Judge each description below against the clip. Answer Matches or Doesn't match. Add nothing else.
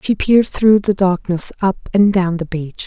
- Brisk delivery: Matches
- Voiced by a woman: Matches